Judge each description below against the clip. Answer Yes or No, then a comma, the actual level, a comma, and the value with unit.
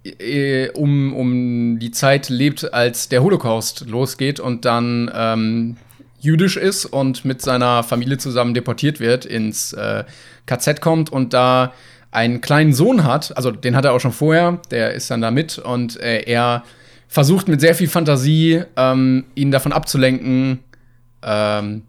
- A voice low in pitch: Yes, low, 130 Hz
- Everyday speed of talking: Yes, average, 155 wpm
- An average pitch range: Yes, average, 3.3 semitones